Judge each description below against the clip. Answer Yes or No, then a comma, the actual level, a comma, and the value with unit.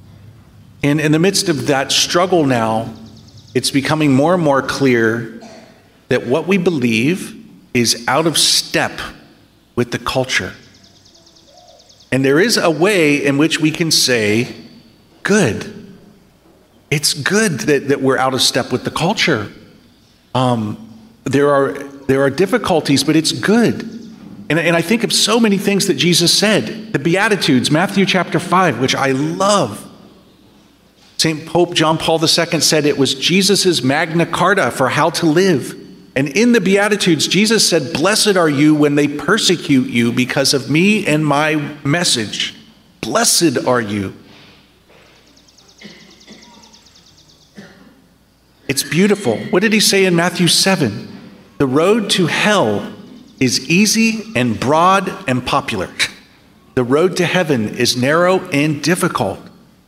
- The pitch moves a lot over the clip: Yes, wide, 5.7 semitones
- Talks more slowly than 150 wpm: Yes, average, 140 wpm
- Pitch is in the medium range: Yes, medium, 155 Hz